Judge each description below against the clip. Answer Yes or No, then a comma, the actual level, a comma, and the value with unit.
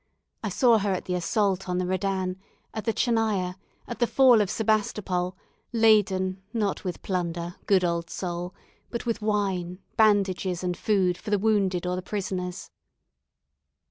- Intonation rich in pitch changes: No, average, 2.8 semitones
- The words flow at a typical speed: Yes, average, 155 wpm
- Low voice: No, high, 190 Hz